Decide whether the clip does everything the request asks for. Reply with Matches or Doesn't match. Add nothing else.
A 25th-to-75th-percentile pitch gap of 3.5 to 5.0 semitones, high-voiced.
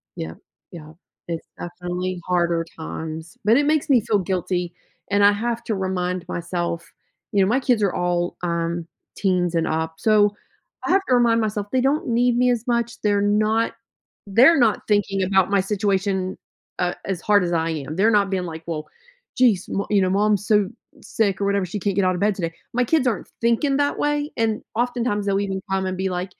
Matches